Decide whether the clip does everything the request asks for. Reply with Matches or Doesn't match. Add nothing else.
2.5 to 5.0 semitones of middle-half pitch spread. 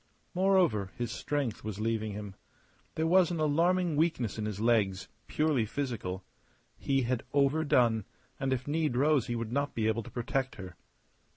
Doesn't match